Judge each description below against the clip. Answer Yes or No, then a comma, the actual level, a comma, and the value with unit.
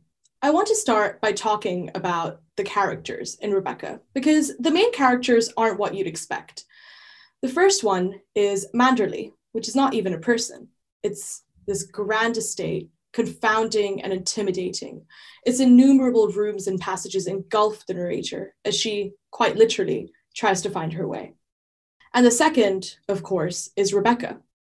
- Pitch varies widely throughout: No, average, 3.9 semitones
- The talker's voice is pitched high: Yes, high, 210 Hz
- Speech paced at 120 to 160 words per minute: Yes, average, 150 wpm